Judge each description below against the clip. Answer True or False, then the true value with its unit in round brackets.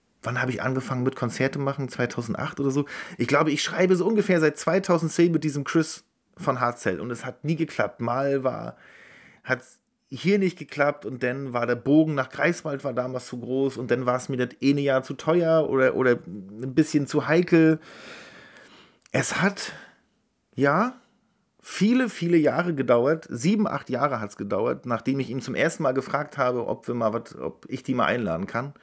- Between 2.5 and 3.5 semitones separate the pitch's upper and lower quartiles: False (4.2 semitones)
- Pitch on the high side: False (140 Hz)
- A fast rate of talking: True (195 wpm)